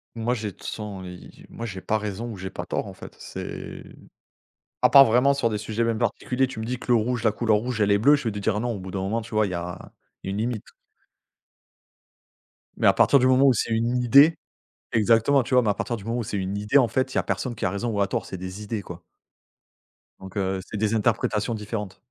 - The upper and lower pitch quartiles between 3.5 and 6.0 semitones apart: No, average, 3.1 semitones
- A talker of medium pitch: No, low, 110 Hz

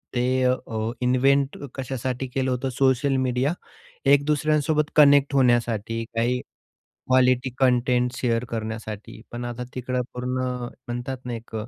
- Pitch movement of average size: No, narrow, 1.8 semitones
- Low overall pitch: Yes, low, 125 Hz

